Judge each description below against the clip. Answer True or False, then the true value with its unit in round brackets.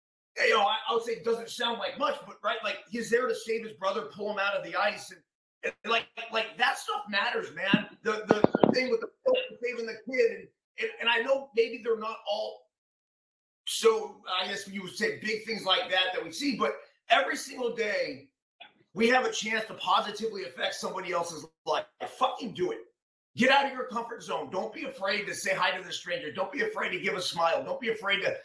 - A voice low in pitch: False (230 Hz)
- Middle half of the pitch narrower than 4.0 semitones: False (5.4 semitones)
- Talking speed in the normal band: False (230 wpm)